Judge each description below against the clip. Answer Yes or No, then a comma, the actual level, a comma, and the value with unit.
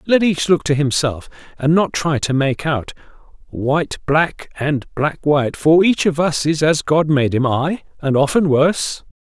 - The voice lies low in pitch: No, medium, 150 Hz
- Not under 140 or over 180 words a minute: No, average, 190 wpm